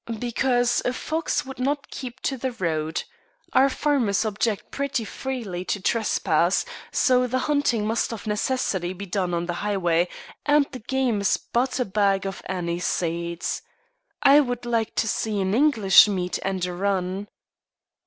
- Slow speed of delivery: No, average, 160 wpm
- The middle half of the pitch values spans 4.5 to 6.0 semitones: Yes, average, 5.3 semitones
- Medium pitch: No, high, 215 Hz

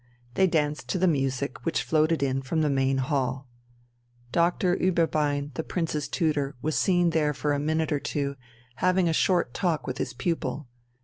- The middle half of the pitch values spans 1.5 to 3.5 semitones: Yes, average, 3.1 semitones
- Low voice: No, medium, 150 Hz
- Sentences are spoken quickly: No, average, 175 wpm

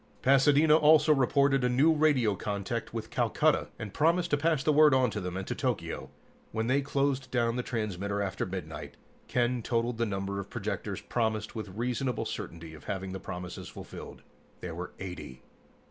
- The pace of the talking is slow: No, average, 175 wpm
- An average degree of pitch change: No, wide, 6.0 semitones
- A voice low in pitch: Yes, low, 115 Hz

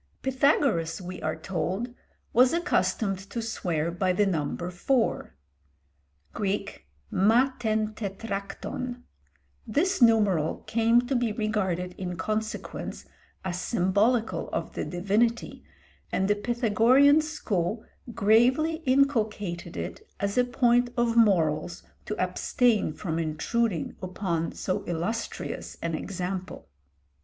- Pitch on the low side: No, high, 210 Hz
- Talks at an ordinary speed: No, slow, 110 wpm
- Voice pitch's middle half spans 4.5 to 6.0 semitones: Yes, average, 4.8 semitones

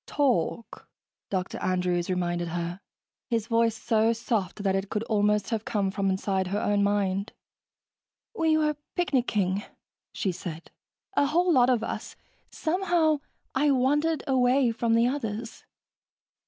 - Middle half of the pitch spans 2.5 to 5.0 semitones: No, wide, 5.4 semitones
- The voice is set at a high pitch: Yes, high, 225 Hz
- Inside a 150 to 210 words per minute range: No, slow, 135 wpm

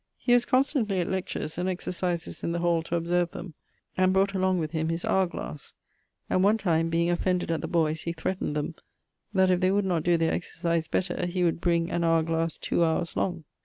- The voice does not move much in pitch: Yes, narrow, 2.1 semitones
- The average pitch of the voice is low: No, medium, 175 Hz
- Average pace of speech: No, fast, 220 wpm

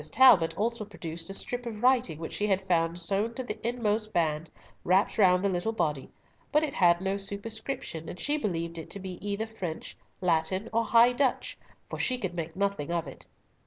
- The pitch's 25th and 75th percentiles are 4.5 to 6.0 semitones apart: Yes, average, 4.8 semitones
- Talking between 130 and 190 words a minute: No, average, 200 wpm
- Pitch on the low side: No, high, 195 Hz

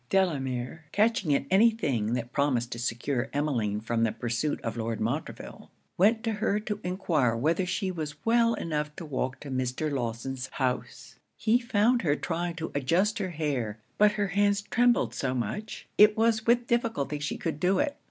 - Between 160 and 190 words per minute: Yes, average, 180 wpm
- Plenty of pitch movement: Yes, wide, 8.5 semitones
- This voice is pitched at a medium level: Yes, medium, 155 Hz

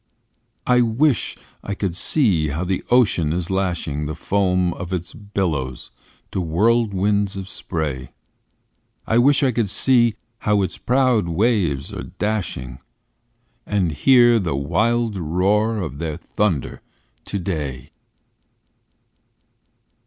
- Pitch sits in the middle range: No, very low, 95 Hz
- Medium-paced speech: No, slow, 115 wpm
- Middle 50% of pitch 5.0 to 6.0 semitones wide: Yes, average, 5.3 semitones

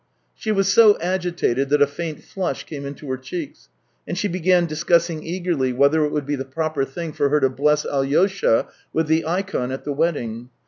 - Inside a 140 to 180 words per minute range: No, average, 195 wpm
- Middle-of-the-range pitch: Yes, medium, 155 Hz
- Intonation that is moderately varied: Yes, average, 3.9 semitones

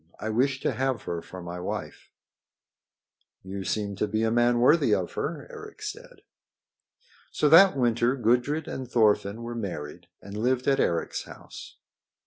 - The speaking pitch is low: Yes, low, 120 Hz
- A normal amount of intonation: Yes, average, 4.6 semitones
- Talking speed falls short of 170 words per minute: Yes, average, 155 wpm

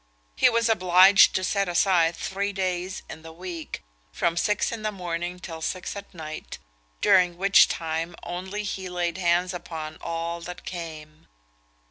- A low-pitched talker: No, medium, 180 Hz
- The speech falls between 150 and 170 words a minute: Yes, average, 155 wpm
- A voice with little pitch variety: Yes, narrow, 2.3 semitones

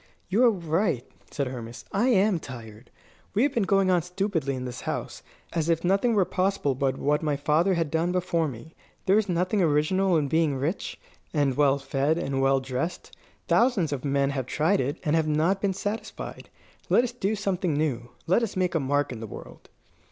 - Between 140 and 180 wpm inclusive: No, average, 200 wpm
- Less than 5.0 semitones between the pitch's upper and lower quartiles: No, wide, 5.6 semitones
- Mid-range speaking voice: Yes, medium, 160 Hz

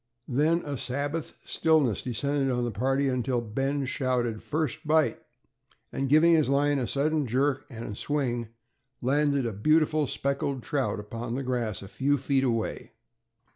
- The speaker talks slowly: No, average, 150 wpm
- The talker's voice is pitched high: No, low, 135 Hz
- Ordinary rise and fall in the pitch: Yes, average, 3.1 semitones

